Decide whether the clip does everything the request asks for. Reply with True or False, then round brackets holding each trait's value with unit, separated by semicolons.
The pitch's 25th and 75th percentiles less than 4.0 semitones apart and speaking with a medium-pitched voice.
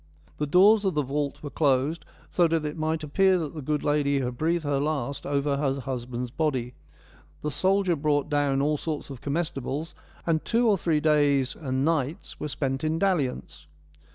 True (2.8 semitones; 150 Hz)